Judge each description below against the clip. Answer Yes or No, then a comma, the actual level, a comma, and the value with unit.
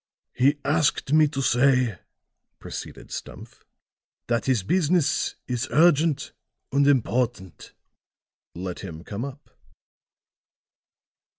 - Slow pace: Yes, slow, 95 wpm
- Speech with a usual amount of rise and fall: Yes, average, 3.8 semitones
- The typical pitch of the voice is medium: No, low, 130 Hz